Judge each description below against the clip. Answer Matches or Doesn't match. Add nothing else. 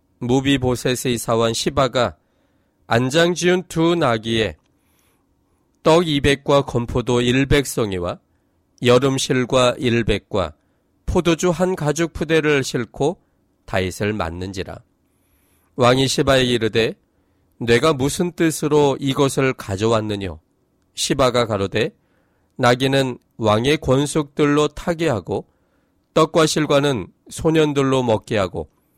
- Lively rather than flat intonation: Matches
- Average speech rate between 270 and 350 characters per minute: Doesn't match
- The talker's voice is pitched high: Doesn't match